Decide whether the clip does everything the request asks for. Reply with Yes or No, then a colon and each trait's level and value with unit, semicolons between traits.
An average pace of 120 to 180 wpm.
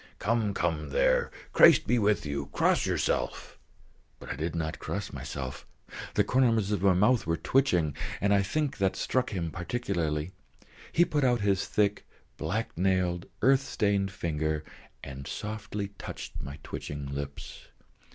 Yes: average, 150 wpm